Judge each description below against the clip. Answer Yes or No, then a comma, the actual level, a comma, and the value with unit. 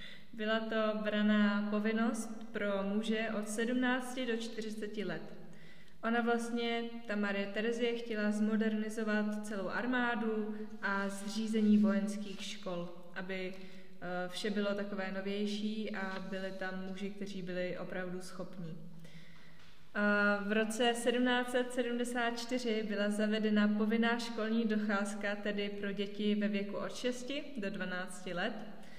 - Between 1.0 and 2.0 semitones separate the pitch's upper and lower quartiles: No, narrow, 2.4 semitones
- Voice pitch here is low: No, high, 210 Hz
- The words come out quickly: No, slow, 115 wpm